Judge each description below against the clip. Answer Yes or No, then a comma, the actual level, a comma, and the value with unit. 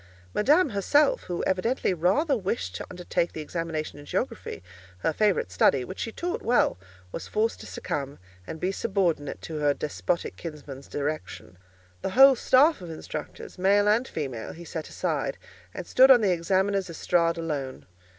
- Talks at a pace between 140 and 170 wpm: Yes, average, 155 wpm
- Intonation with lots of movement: Yes, wide, 6.3 semitones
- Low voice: No, medium, 175 Hz